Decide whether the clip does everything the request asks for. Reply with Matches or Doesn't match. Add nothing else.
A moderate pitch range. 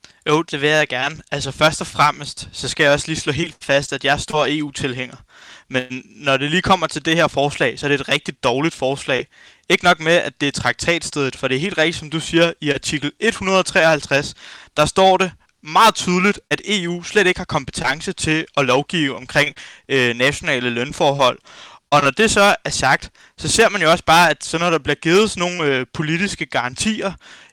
Matches